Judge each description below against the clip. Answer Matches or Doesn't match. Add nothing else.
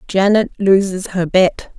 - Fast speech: Doesn't match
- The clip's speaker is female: Matches